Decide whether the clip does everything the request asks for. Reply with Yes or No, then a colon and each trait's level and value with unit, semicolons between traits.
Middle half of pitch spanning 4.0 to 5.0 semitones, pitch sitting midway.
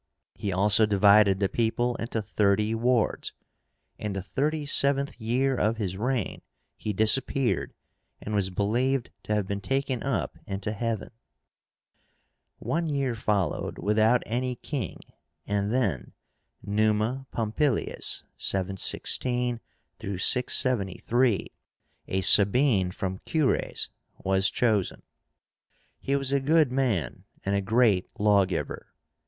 No: average, 4.3 semitones; low, 110 Hz